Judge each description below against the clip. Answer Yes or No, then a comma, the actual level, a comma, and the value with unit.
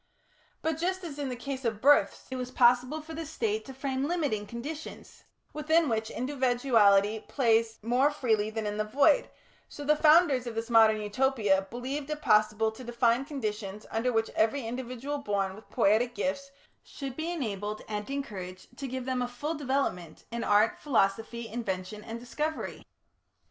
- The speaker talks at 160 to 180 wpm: Yes, average, 170 wpm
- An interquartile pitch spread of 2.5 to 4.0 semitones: No, average, 4.4 semitones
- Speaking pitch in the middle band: No, high, 245 Hz